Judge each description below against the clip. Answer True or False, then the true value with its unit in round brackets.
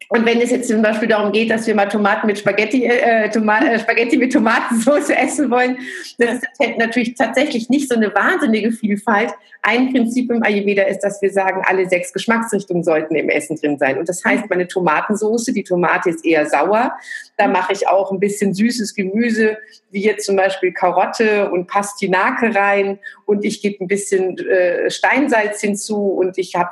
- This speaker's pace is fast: True (195 wpm)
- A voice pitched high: True (210 Hz)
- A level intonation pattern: False (3.3 semitones)